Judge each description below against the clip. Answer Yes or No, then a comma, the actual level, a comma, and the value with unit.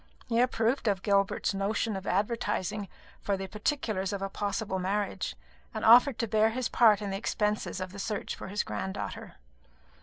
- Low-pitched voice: No, high, 205 Hz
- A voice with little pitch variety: Yes, narrow, 2.3 semitones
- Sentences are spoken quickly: No, average, 175 wpm